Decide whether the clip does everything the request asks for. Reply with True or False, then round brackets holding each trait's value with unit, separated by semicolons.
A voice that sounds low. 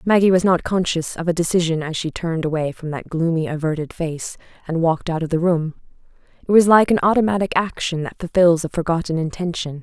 False (170 Hz)